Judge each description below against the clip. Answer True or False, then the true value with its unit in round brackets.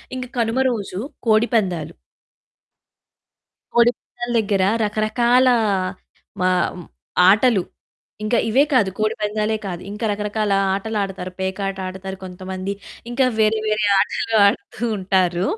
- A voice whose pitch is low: False (210 Hz)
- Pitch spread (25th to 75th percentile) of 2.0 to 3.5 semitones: True (2.8 semitones)